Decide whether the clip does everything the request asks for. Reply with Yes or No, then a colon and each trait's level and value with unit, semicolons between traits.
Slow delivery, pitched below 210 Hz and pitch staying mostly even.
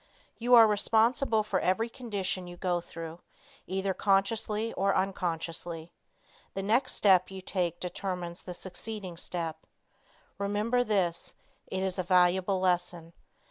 No: slow, 130 wpm; high, 190 Hz; average, 3.1 semitones